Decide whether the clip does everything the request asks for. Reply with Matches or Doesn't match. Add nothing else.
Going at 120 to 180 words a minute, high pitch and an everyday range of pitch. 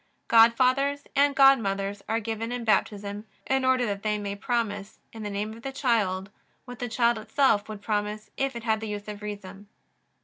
Doesn't match